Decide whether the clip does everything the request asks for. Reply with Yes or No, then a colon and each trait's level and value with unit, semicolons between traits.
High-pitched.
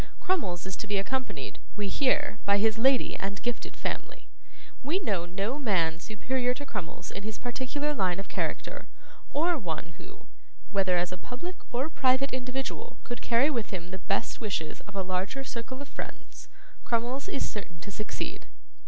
Yes: high, 225 Hz